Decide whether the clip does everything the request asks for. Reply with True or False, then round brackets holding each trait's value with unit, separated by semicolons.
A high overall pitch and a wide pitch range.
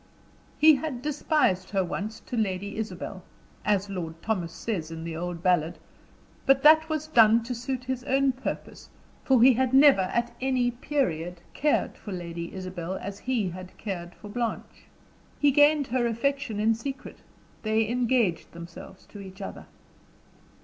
True (220 Hz; 6.0 semitones)